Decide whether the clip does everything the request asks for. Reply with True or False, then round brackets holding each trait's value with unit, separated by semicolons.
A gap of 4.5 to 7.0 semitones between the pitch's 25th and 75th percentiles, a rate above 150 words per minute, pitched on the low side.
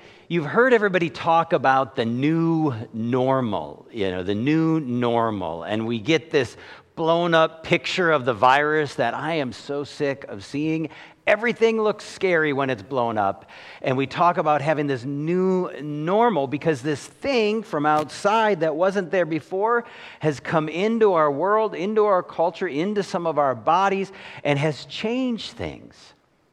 False (5.2 semitones; 160 wpm; 155 Hz)